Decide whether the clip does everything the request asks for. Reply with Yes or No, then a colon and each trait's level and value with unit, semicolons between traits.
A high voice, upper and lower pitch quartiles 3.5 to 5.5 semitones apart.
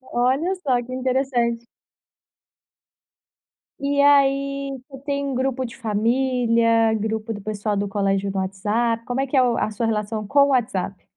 Yes: high, 235 Hz; average, 3.8 semitones